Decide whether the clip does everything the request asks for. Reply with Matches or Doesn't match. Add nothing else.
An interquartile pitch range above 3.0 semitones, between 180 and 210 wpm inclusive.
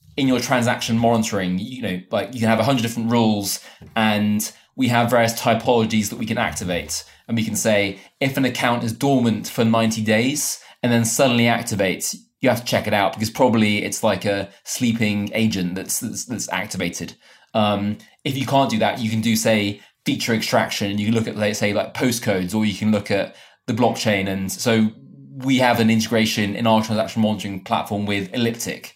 Doesn't match